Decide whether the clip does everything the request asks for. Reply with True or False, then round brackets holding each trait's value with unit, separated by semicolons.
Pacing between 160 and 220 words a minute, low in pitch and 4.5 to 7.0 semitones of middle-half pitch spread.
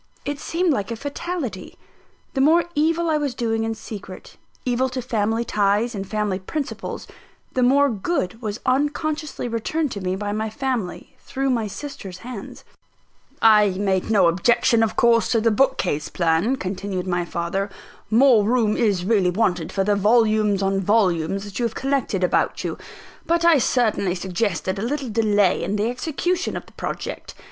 False (170 wpm; 220 Hz; 5.1 semitones)